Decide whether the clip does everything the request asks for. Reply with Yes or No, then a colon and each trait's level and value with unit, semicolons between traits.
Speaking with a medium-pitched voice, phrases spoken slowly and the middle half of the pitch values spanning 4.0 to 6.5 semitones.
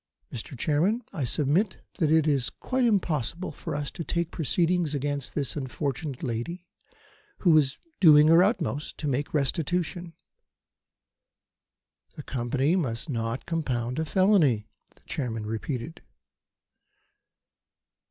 Yes: medium, 150 Hz; slow, 120 wpm; average, 4.4 semitones